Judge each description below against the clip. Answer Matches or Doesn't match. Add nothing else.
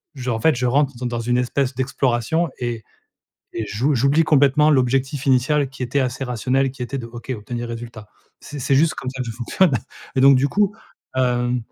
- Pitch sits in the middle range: Doesn't match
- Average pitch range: Doesn't match